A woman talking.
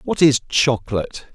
No: male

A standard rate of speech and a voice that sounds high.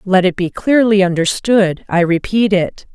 Yes: average, 165 wpm; high, 195 Hz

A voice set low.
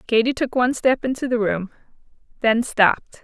No: high, 240 Hz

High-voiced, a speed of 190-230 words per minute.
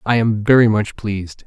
No: low, 105 Hz; fast, 205 wpm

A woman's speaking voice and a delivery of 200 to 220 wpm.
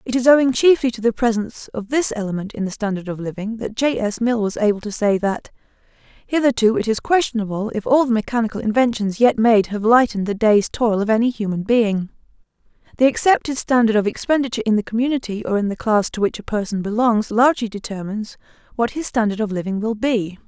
Yes: female; fast, 205 wpm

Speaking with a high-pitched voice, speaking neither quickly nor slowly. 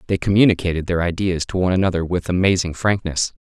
No: very low, 90 Hz; average, 175 wpm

